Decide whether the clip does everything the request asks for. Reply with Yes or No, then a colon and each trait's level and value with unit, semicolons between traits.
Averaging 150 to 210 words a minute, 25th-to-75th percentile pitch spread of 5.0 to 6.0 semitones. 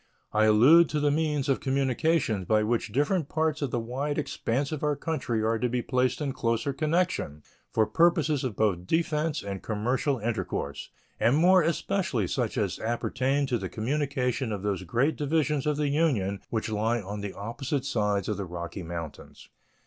Yes: average, 180 wpm; wide, 5.6 semitones